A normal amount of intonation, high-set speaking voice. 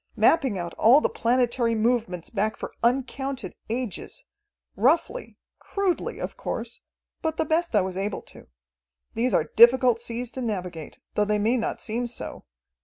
Yes: average, 3.6 semitones; high, 235 Hz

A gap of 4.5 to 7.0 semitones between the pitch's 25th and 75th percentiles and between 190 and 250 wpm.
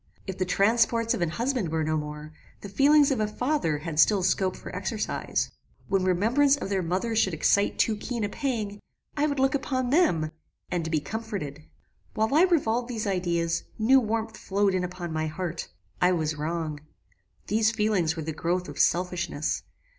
No: wide, 5.5 semitones; average, 180 wpm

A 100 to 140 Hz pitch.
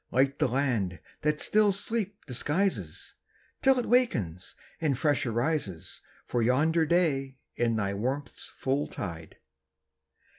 Yes: low, 135 Hz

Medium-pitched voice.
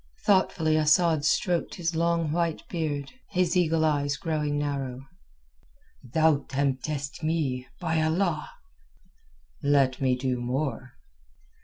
Yes: medium, 155 Hz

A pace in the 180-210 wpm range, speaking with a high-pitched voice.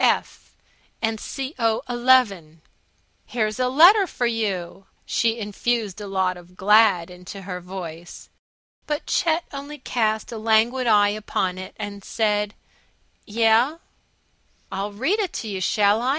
No: slow, 135 wpm; high, 215 Hz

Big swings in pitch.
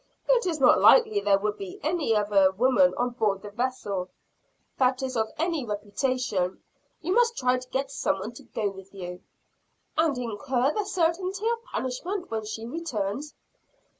Yes: wide, 7.5 semitones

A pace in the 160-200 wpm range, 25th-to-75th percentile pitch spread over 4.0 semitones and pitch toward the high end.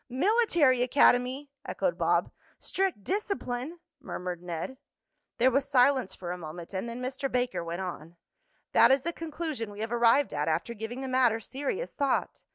Yes: average, 165 wpm; wide, 5.6 semitones; very high, 250 Hz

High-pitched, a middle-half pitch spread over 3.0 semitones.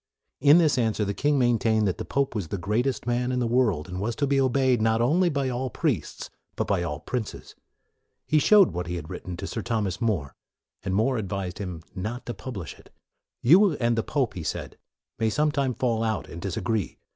No: low, 115 Hz; average, 5.0 semitones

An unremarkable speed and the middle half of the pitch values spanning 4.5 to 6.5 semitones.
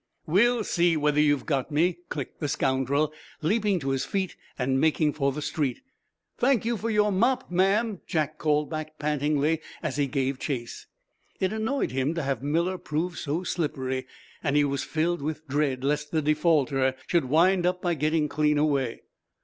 No: average, 175 wpm; average, 3.8 semitones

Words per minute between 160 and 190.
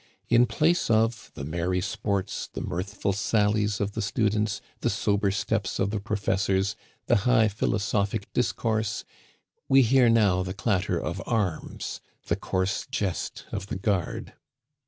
No: average, 140 wpm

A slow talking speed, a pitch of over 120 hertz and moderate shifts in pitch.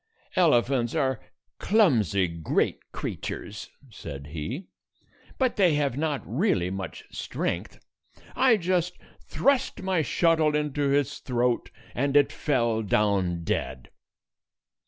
No: slow, 110 wpm; medium, 140 Hz; wide, 8.0 semitones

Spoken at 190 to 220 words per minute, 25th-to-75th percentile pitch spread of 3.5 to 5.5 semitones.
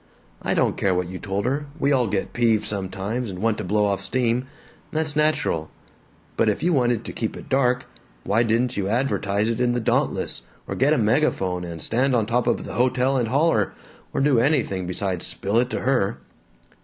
Yes: fast, 205 wpm; average, 4.4 semitones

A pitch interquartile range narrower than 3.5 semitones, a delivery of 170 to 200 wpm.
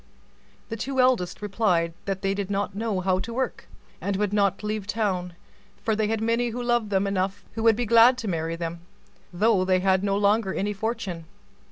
Yes: average, 3.1 semitones; average, 185 wpm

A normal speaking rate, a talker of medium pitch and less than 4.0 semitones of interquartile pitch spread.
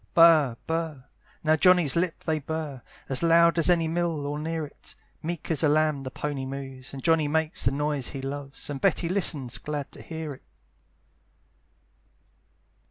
Yes: average, 165 wpm; medium, 155 Hz; average, 2.9 semitones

